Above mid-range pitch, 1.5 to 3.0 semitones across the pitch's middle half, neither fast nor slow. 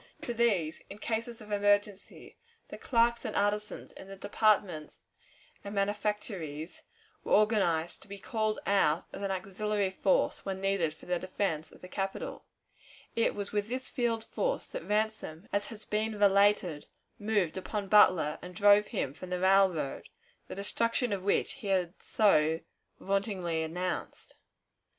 Yes: high, 200 Hz; average, 2.7 semitones; average, 150 wpm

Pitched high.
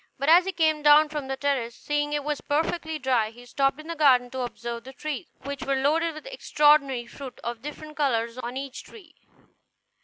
Yes: very high, 280 Hz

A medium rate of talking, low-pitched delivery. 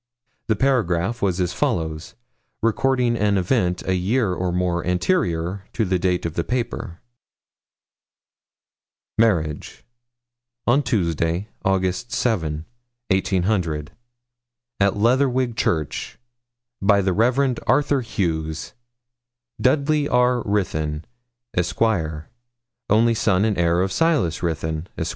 No: slow, 105 wpm; very low, 95 Hz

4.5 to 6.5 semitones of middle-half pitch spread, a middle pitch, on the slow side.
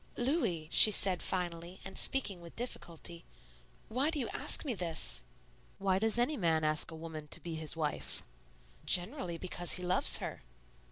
No: average, 5.1 semitones; medium, 180 Hz; average, 165 wpm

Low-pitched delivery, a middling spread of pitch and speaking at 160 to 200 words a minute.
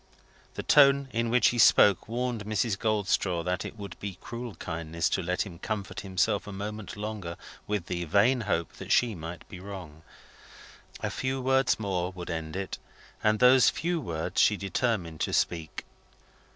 Yes: low, 100 Hz; average, 4.7 semitones; average, 170 wpm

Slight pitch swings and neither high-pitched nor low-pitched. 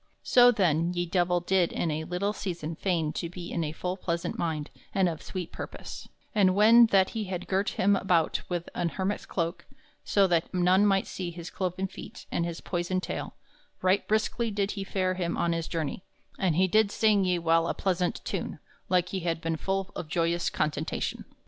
Yes: narrow, 2.3 semitones; medium, 180 Hz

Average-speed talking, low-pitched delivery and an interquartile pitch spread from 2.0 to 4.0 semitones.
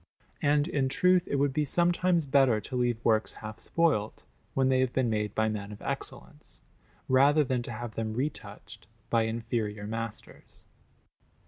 No: average, 160 wpm; low, 125 Hz; average, 4.5 semitones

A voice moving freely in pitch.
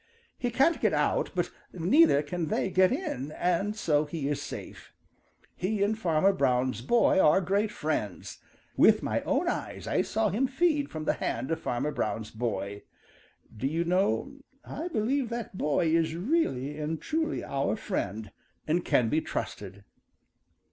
Yes: wide, 7.6 semitones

